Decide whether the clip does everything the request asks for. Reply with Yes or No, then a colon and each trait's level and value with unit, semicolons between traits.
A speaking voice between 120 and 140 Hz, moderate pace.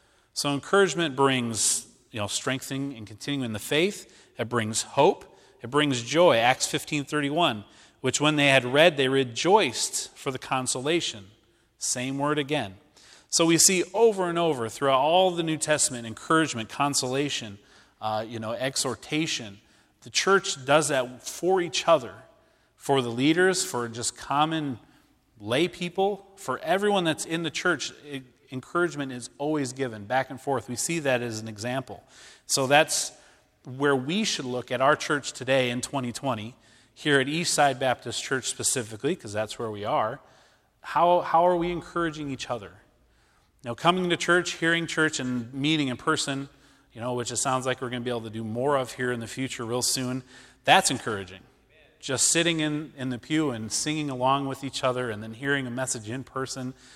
Yes: low, 135 Hz; average, 175 wpm